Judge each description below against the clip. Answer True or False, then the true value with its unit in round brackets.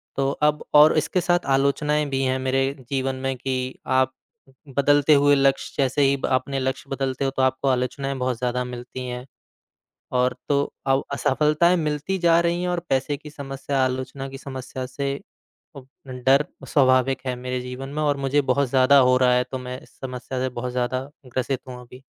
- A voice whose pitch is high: False (135 Hz)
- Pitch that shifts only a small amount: True (1.7 semitones)